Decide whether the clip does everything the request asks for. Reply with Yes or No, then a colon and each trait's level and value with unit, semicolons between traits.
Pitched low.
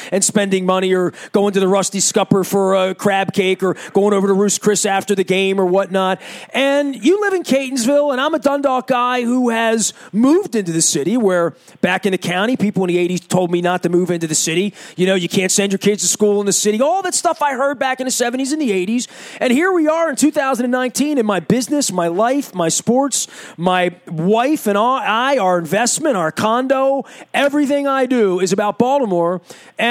No: high, 205 Hz